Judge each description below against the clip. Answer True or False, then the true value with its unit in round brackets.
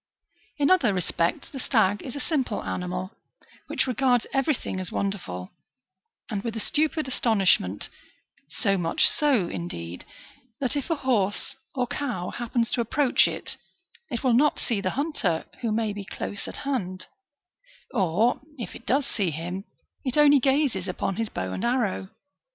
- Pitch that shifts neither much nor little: False (6.2 semitones)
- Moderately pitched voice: False (225 Hz)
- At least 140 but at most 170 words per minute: True (160 wpm)